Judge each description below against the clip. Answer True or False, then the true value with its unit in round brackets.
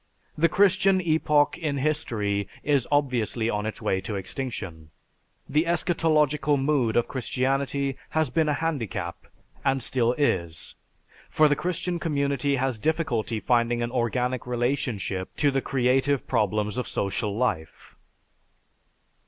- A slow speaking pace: True (130 wpm)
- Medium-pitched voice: False (130 Hz)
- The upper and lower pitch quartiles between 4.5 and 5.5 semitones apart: True (4.8 semitones)